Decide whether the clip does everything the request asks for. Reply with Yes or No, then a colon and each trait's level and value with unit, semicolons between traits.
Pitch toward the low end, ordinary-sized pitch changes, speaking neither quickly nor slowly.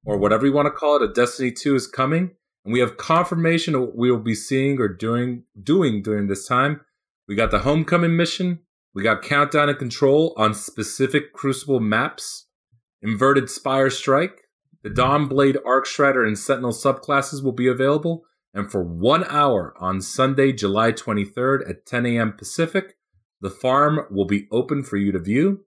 Yes: low, 130 Hz; average, 4.8 semitones; average, 180 wpm